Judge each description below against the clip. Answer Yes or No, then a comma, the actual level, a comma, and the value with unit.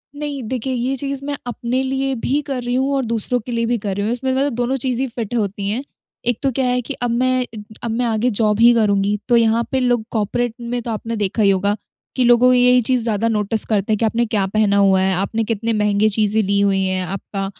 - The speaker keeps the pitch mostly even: No, average, 3.2 semitones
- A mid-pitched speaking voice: No, high, 230 Hz